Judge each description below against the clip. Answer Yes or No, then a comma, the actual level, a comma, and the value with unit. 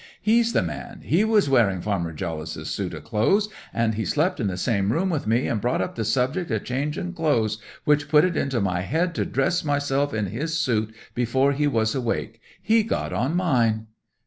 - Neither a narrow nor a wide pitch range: No, wide, 6.6 semitones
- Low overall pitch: Yes, low, 125 Hz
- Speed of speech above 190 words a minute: Yes, average, 200 wpm